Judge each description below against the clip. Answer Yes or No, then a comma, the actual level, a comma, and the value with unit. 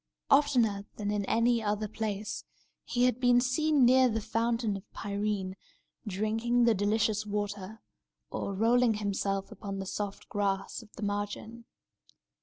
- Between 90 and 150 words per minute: Yes, average, 140 wpm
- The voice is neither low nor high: No, high, 215 Hz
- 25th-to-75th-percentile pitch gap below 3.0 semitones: Yes, narrow, 2.6 semitones